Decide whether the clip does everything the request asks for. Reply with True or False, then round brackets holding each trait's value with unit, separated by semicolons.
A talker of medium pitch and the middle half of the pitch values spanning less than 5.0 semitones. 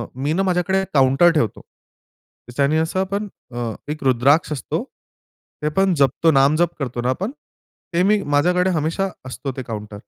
False (150 Hz; 5.3 semitones)